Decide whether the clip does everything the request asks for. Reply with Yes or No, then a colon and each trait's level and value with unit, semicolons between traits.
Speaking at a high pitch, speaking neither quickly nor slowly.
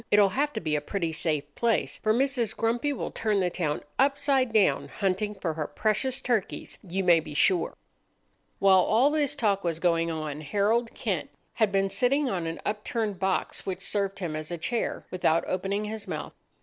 Yes: high, 200 Hz; average, 190 wpm